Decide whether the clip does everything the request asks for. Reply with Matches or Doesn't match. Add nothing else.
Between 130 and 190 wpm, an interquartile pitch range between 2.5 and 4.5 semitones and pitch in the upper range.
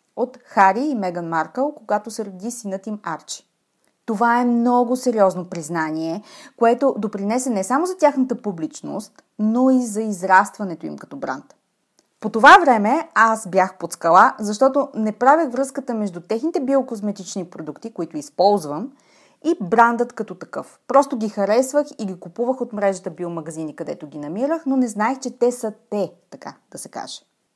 Doesn't match